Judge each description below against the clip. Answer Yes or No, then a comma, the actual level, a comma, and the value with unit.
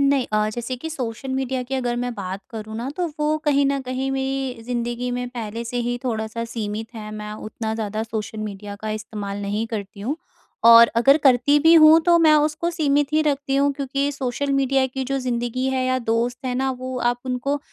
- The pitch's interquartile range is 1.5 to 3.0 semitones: No, average, 3.4 semitones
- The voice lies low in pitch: No, very high, 250 Hz